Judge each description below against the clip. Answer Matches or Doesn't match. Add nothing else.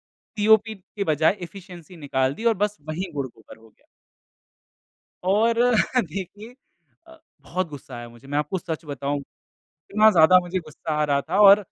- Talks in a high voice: Doesn't match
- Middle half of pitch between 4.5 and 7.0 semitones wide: Matches